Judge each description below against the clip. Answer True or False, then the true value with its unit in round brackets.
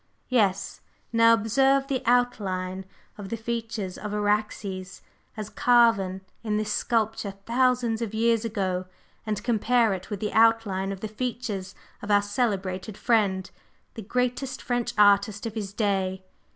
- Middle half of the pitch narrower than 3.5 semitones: True (3.0 semitones)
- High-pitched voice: True (215 Hz)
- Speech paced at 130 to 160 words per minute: True (140 wpm)